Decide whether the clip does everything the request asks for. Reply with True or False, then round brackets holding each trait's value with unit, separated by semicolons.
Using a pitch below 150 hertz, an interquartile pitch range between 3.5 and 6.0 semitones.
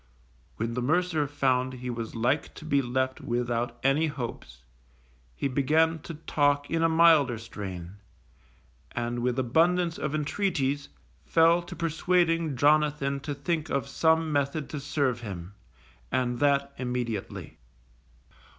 True (140 Hz; 4.5 semitones)